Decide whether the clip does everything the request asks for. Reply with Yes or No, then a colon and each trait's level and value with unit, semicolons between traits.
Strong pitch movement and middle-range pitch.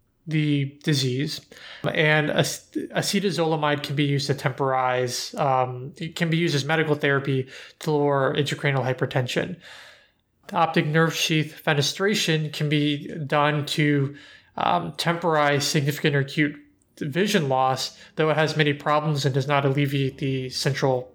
No: narrow, 2.4 semitones; medium, 145 Hz